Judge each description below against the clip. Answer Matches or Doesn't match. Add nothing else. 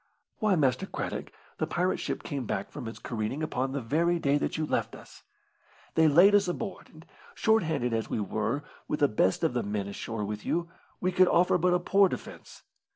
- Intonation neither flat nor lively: Doesn't match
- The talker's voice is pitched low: Doesn't match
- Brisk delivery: Matches